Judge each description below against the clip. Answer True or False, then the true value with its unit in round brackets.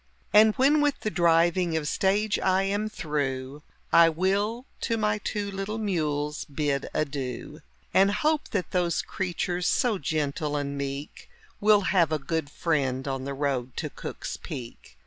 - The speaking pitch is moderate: True (170 Hz)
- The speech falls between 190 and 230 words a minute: False (155 wpm)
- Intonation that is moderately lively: False (6.0 semitones)